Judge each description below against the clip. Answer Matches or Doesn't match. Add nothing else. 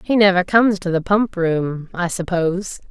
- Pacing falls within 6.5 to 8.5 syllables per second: Doesn't match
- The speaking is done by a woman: Matches